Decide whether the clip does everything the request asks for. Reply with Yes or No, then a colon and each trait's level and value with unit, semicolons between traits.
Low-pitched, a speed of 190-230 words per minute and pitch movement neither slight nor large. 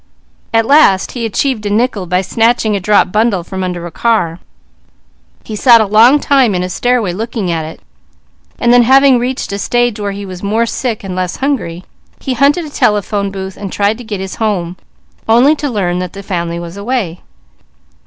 No: high, 210 Hz; average, 195 wpm; average, 4.6 semitones